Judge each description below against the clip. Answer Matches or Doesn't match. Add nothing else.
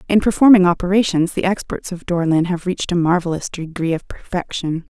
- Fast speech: Doesn't match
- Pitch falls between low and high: Matches